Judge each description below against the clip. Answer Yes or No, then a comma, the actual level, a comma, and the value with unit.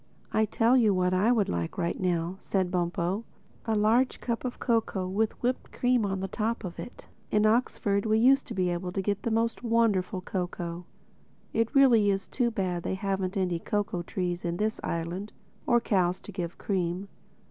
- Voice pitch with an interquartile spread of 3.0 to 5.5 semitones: Yes, average, 3.8 semitones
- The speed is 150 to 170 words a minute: No, average, 185 wpm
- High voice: Yes, high, 200 Hz